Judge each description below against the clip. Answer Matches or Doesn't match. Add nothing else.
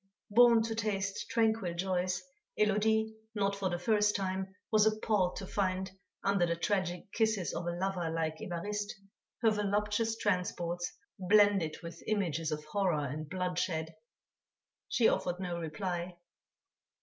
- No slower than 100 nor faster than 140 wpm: Matches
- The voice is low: Doesn't match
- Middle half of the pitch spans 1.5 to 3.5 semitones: Matches